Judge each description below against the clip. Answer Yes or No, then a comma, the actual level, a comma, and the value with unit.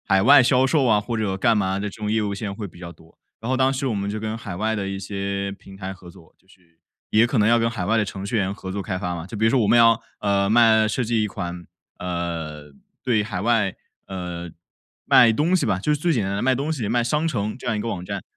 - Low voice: Yes, low, 105 Hz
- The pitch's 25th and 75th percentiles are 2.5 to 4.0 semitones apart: Yes, average, 3.4 semitones